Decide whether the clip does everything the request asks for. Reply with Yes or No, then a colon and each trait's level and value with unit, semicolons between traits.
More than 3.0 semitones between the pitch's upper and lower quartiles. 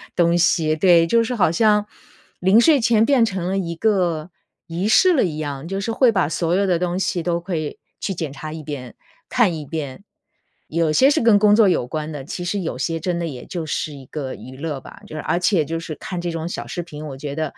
Yes: average, 4.0 semitones